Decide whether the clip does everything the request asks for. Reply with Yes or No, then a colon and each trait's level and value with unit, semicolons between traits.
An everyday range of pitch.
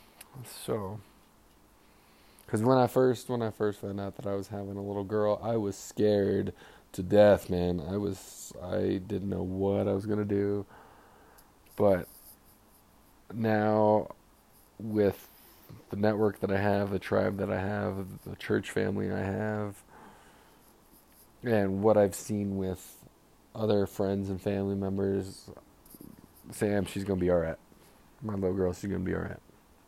No: narrow, 1.7 semitones